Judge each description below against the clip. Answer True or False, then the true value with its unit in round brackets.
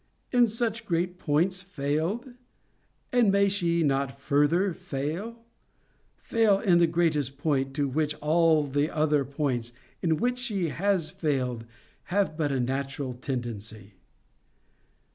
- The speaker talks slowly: True (125 wpm)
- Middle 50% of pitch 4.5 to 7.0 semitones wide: True (5.6 semitones)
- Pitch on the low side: False (155 Hz)